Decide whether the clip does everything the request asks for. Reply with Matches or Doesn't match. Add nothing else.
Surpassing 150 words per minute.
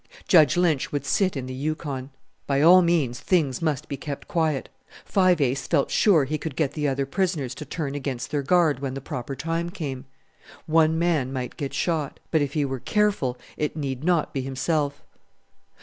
Matches